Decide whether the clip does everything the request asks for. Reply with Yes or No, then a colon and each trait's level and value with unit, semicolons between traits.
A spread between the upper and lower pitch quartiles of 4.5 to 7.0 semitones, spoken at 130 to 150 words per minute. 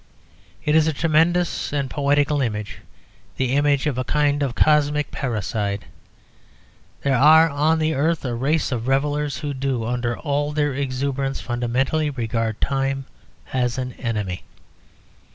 No: average, 3.2 semitones; average, 140 wpm